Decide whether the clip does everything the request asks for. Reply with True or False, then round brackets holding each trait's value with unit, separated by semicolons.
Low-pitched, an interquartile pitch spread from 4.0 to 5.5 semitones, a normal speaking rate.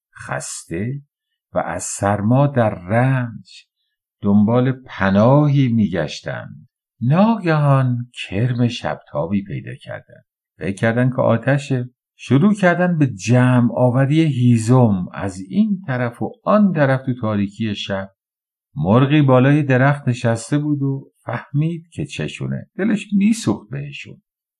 False (125 Hz; 4.7 semitones; 105 wpm)